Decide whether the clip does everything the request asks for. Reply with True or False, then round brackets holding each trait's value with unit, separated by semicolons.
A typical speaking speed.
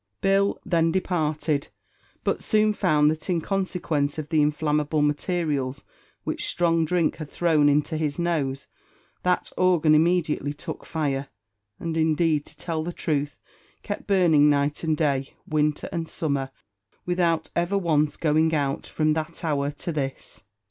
True (145 wpm)